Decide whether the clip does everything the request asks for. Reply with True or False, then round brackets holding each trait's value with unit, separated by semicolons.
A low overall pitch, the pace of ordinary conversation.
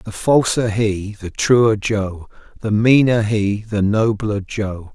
True (105 Hz; 145 wpm)